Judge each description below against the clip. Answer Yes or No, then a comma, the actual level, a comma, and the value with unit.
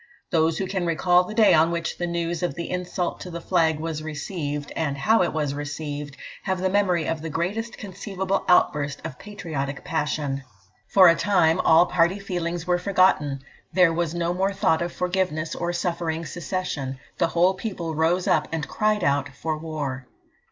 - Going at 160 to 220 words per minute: Yes, average, 180 wpm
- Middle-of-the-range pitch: Yes, medium, 170 Hz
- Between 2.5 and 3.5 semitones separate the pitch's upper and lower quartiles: Yes, average, 2.8 semitones